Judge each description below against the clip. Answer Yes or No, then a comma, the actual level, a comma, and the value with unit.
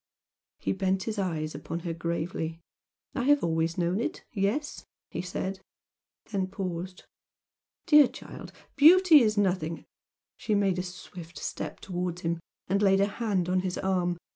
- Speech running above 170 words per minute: No, average, 155 wpm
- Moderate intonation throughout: Yes, average, 3.1 semitones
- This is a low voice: No, medium, 185 Hz